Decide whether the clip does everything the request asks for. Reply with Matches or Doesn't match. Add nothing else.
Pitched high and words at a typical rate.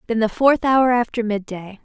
Matches